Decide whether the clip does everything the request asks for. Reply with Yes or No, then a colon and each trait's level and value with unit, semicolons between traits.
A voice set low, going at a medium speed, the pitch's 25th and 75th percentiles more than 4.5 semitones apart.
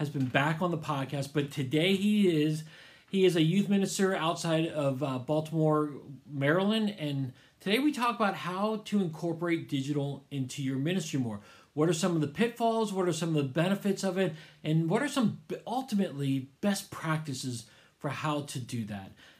No: medium, 155 Hz; average, 185 wpm; average, 5.2 semitones